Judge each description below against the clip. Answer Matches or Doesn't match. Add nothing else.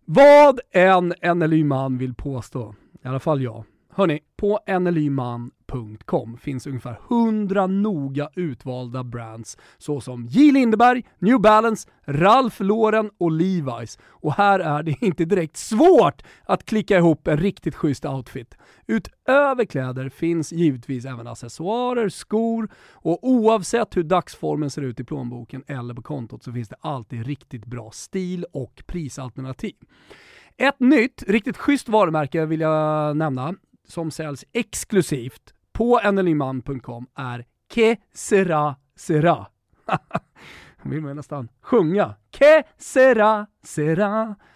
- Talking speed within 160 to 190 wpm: Doesn't match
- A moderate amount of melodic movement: Doesn't match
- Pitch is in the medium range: Matches